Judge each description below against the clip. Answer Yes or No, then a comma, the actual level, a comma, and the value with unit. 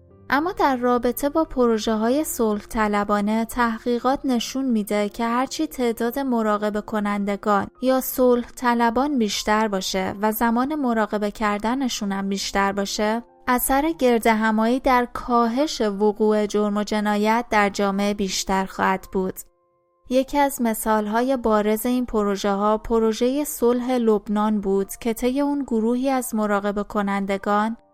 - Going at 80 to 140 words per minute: Yes, average, 125 wpm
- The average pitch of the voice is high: Yes, high, 225 Hz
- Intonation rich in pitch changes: No, average, 3.1 semitones